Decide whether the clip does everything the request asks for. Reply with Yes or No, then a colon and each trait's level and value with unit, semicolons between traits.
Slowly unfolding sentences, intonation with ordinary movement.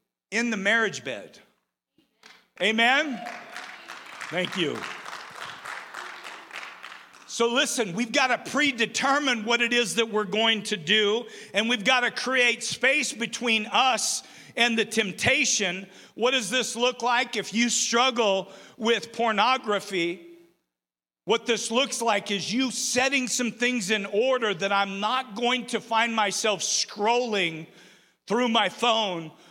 Yes: slow, 130 wpm; average, 3.1 semitones